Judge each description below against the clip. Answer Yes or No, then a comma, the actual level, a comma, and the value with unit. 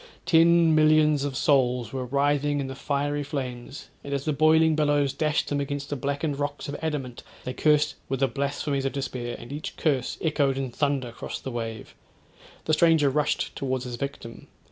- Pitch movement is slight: Yes, narrow, 2.2 semitones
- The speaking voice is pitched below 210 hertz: Yes, medium, 140 Hz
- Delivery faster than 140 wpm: Yes, average, 185 wpm